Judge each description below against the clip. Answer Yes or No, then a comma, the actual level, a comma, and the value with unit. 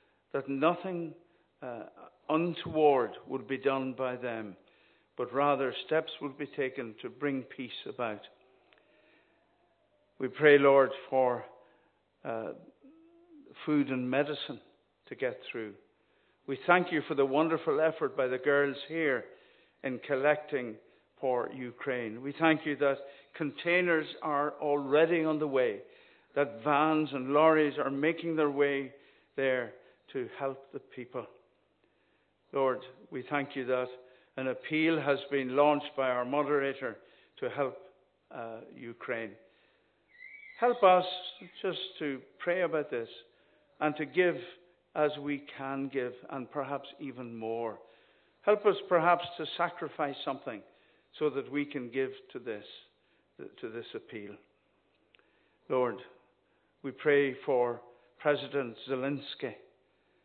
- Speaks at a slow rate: Yes, slow, 125 wpm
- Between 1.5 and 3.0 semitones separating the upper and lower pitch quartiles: No, average, 4.0 semitones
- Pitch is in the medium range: Yes, medium, 145 Hz